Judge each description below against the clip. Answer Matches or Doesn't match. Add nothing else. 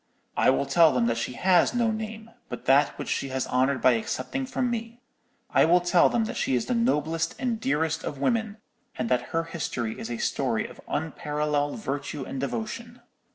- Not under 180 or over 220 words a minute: Matches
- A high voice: Doesn't match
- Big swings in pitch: Matches